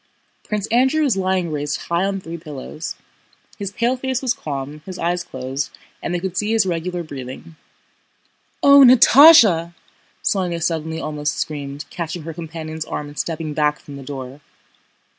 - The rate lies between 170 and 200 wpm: No, average, 160 wpm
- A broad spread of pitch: No, average, 4.5 semitones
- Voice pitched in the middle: Yes, medium, 170 Hz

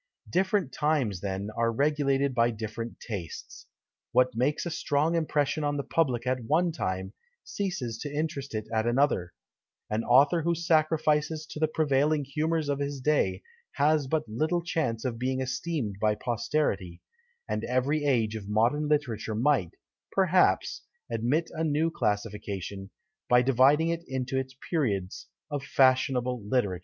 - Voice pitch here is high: No, low, 135 Hz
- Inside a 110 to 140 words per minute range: No, average, 150 wpm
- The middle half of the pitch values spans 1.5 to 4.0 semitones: No, average, 5.0 semitones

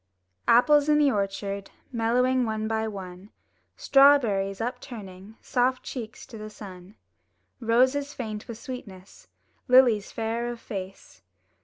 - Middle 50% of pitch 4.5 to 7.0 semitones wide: No, average, 4.1 semitones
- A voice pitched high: Yes, high, 225 Hz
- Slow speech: Yes, slow, 120 wpm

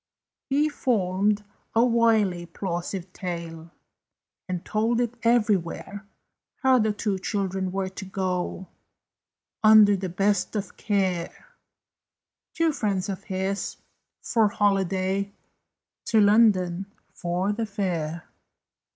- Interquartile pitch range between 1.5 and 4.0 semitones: Yes, average, 2.7 semitones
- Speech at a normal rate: No, slow, 105 wpm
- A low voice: No, high, 195 Hz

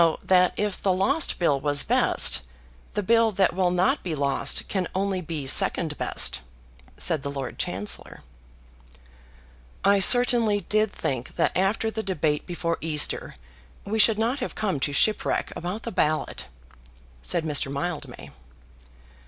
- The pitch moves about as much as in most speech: No, wide, 5.8 semitones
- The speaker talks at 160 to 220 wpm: No, average, 145 wpm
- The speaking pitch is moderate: Yes, medium, 180 Hz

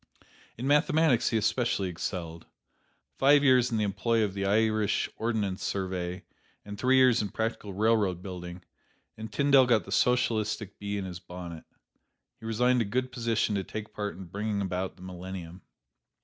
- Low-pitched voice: Yes, low, 105 Hz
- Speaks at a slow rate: No, average, 165 wpm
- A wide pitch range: No, average, 3.9 semitones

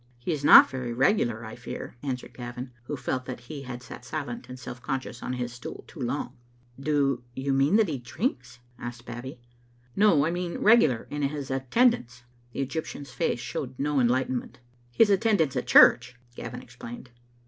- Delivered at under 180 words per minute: No, average, 185 wpm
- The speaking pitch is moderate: No, low, 130 Hz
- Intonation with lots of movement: No, average, 3.2 semitones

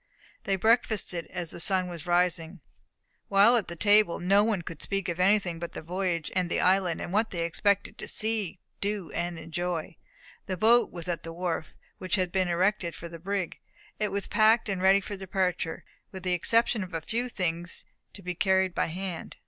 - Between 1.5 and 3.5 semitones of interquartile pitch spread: Yes, average, 2.8 semitones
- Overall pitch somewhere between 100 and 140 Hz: No, medium, 185 Hz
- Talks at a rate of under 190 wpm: No, average, 195 wpm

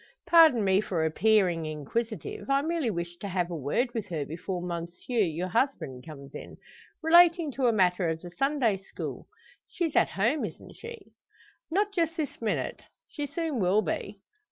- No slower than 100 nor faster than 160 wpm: No, average, 170 wpm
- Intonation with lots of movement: Yes, wide, 8.7 semitones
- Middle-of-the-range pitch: No, high, 210 Hz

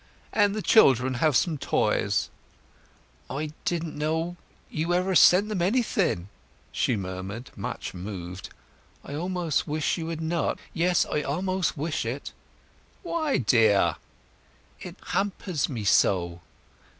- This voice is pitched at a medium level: Yes, medium, 155 Hz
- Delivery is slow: Yes, slow, 115 wpm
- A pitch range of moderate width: No, wide, 7.3 semitones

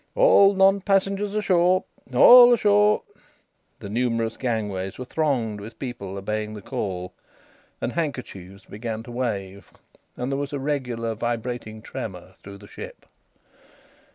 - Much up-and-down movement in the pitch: Yes, wide, 8.4 semitones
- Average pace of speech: No, slow, 130 wpm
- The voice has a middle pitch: No, low, 120 Hz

